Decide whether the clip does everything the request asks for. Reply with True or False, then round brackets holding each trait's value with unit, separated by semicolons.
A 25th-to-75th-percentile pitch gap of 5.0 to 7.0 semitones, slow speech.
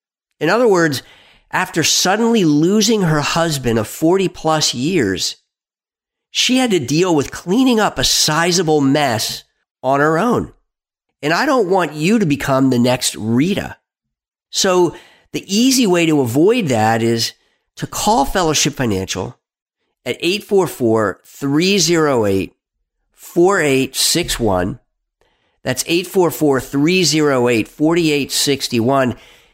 True (5.6 semitones; 105 wpm)